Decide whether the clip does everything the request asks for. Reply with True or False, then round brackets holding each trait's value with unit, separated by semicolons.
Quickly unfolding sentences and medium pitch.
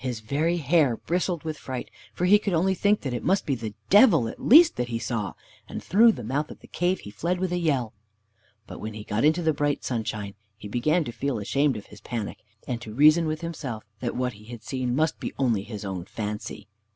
False (235 wpm; 130 Hz)